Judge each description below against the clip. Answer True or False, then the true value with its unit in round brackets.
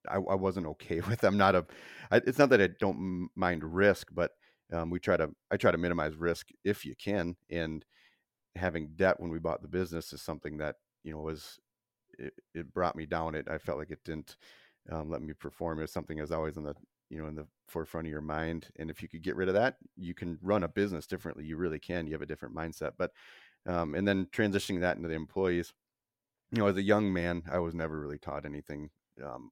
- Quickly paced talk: True (240 wpm)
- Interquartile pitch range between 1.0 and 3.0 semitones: True (2.5 semitones)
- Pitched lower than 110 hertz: True (85 Hz)